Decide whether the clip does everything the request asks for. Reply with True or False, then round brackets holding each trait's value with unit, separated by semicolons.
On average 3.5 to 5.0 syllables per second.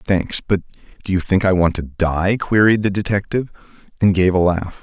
False (5.3 syllables/s)